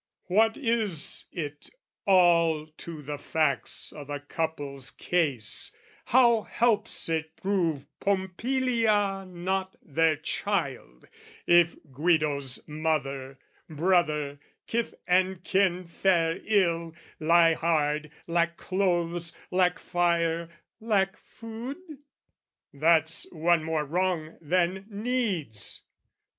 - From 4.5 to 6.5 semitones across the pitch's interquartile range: No, average, 3.7 semitones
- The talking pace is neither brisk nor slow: No, slow, 95 wpm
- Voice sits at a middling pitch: Yes, medium, 170 Hz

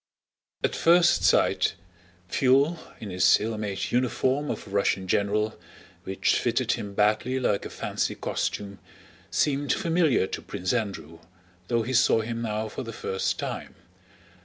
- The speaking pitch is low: Yes, low, 110 Hz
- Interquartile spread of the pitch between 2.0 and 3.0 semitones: No, average, 4.6 semitones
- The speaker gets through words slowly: No, average, 145 wpm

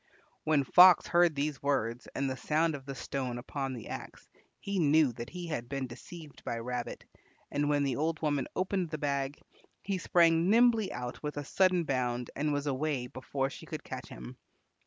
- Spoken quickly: No, average, 190 wpm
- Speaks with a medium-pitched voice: Yes, medium, 145 Hz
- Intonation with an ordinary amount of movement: Yes, average, 4.0 semitones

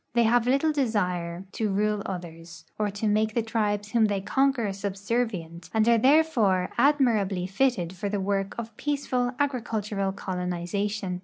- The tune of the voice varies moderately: Yes, average, 3.7 semitones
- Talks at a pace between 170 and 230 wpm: No, average, 155 wpm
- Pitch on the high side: Yes, high, 210 Hz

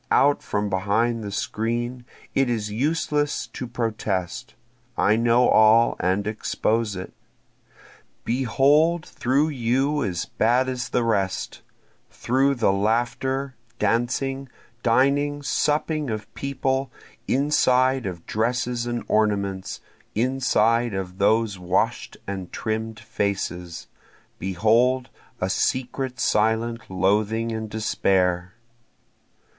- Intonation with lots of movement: No, average, 3.9 semitones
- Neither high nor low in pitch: No, low, 115 Hz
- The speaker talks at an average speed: No, slow, 105 wpm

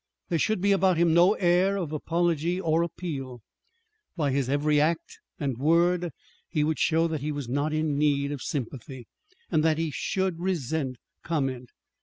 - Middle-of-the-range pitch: Yes, medium, 155 Hz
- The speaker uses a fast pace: No, average, 170 wpm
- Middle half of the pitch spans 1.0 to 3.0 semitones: No, average, 3.4 semitones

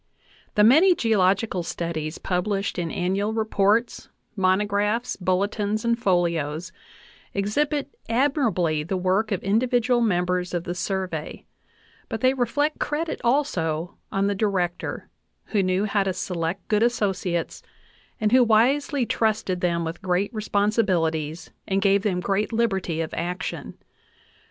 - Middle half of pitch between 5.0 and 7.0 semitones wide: No, average, 4.0 semitones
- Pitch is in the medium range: No, high, 195 Hz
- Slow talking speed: Yes, slow, 130 wpm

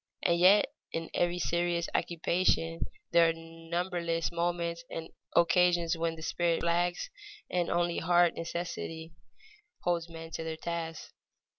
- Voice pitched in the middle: Yes, medium, 170 Hz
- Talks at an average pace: No, slow, 130 wpm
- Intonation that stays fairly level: Yes, narrow, 1.0 semitones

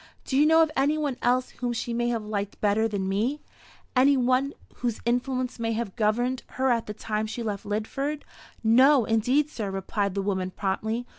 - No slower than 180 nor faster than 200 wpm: Yes, average, 195 wpm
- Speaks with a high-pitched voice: Yes, high, 235 Hz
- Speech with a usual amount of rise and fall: Yes, average, 3.5 semitones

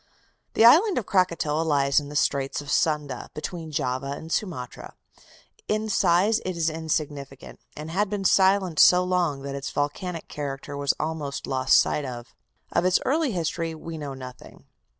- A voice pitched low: No, medium, 155 Hz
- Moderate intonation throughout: Yes, average, 4.5 semitones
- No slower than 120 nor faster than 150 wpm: No, average, 165 wpm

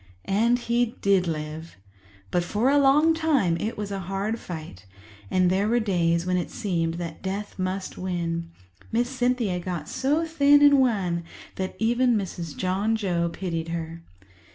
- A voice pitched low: No, high, 195 Hz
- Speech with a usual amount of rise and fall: No, wide, 5.8 semitones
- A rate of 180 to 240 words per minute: No, average, 160 wpm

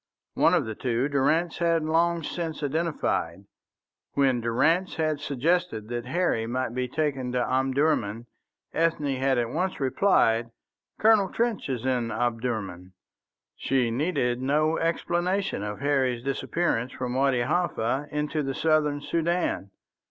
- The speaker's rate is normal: No, slow, 130 wpm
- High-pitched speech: No, low, 135 Hz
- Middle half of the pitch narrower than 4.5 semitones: No, average, 5.1 semitones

